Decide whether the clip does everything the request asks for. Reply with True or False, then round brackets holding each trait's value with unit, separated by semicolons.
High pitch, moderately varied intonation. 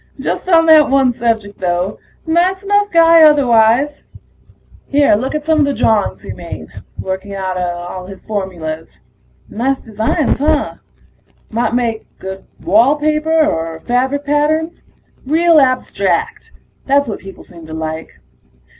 False (250 Hz; 7.8 semitones)